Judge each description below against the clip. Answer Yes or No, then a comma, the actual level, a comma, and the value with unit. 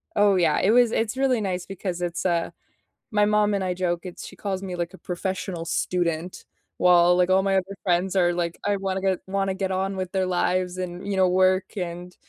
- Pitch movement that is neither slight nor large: No, narrow, 1.6 semitones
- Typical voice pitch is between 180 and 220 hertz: Yes, medium, 185 Hz